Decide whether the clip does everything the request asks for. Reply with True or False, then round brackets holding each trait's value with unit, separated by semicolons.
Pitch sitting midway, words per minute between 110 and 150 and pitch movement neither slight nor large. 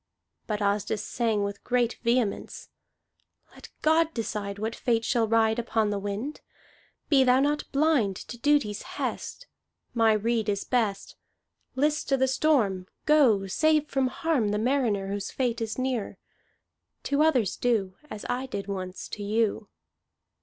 False (230 Hz; 145 wpm; 4.4 semitones)